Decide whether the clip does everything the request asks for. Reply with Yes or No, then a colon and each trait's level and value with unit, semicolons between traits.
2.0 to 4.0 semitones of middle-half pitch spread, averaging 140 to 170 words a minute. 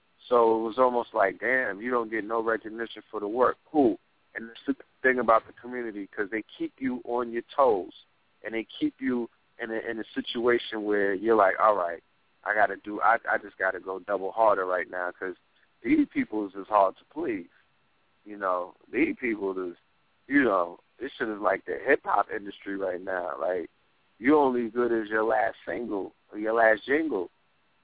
No: average, 2.8 semitones; average, 200 wpm